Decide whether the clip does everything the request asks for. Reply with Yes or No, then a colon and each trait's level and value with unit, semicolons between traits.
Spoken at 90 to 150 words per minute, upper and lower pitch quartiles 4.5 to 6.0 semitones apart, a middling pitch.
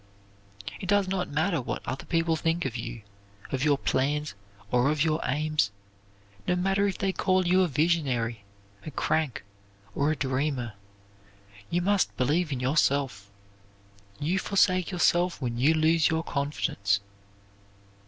Yes: average, 145 wpm; average, 5.1 semitones; medium, 155 Hz